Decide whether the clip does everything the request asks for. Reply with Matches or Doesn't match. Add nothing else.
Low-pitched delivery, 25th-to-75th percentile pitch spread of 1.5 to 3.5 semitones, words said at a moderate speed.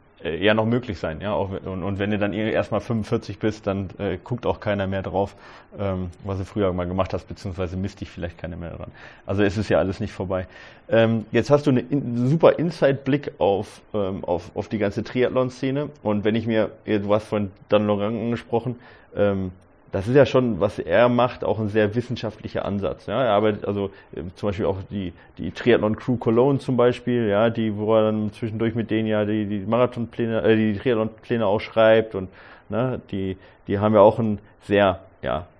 Doesn't match